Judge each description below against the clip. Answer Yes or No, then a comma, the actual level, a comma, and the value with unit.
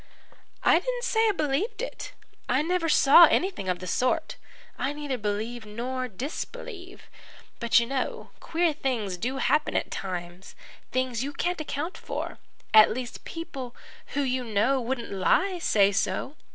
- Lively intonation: Yes, wide, 6.9 semitones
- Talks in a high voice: Yes, very high, 260 Hz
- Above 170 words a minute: No, average, 150 wpm